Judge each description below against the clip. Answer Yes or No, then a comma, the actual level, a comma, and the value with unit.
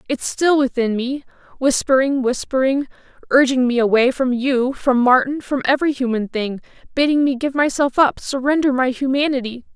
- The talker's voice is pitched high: Yes, very high, 265 Hz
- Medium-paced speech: Yes, average, 150 wpm